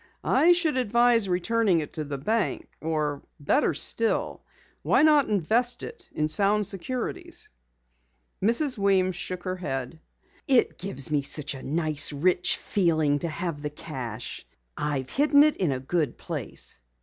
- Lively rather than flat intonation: Yes, wide, 7.5 semitones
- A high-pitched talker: No, medium, 180 Hz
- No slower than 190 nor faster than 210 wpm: No, average, 145 wpm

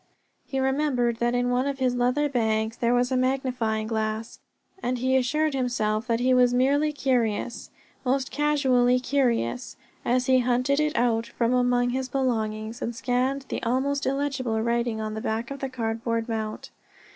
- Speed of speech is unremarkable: Yes, average, 170 wpm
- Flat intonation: Yes, narrow, 2.3 semitones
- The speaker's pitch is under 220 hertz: No, high, 245 Hz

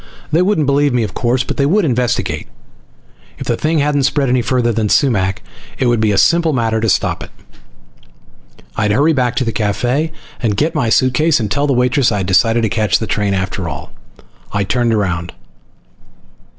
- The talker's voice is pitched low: Yes, low, 120 Hz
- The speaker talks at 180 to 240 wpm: Yes, average, 190 wpm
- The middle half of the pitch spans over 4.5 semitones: Yes, average, 4.9 semitones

